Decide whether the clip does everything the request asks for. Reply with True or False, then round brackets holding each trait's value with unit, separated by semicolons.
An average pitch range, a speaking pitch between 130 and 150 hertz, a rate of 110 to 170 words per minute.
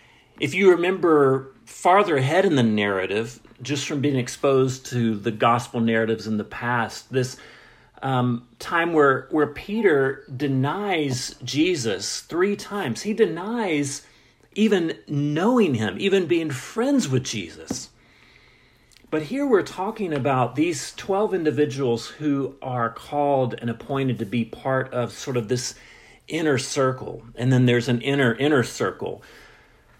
True (4.3 semitones; 135 Hz; 135 wpm)